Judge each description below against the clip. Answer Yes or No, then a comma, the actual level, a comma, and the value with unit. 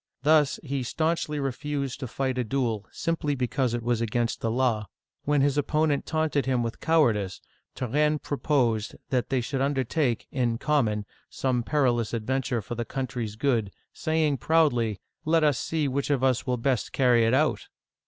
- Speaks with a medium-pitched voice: No, low, 130 Hz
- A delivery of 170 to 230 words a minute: Yes, average, 175 wpm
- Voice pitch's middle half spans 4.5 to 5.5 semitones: No, average, 3.7 semitones